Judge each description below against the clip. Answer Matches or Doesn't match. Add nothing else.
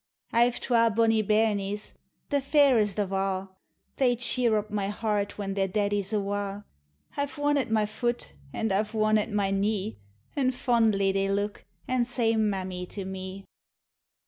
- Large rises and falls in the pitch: Doesn't match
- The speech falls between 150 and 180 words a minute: Matches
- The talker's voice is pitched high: Matches